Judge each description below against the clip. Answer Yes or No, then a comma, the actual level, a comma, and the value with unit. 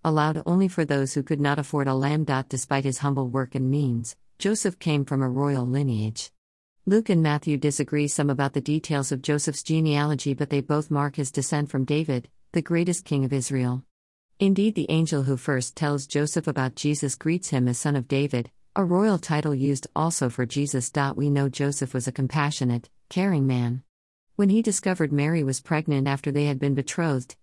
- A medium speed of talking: No, fast, 190 wpm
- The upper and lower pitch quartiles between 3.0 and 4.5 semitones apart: No, narrow, 2.5 semitones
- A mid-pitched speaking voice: Yes, medium, 145 Hz